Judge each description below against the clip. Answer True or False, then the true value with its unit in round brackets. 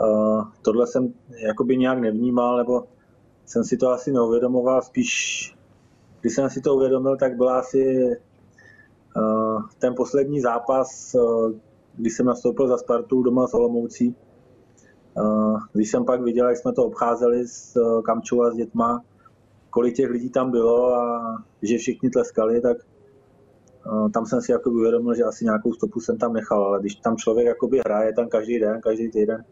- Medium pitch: False (120 Hz)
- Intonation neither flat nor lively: False (2.0 semitones)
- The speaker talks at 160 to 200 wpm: True (165 wpm)